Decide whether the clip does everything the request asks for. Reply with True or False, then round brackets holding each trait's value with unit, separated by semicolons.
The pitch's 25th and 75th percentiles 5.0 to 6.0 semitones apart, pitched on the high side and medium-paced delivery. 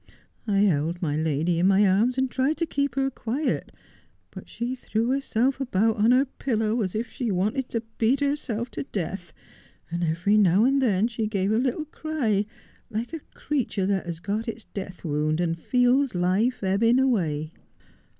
True (5.4 semitones; 220 Hz; 180 wpm)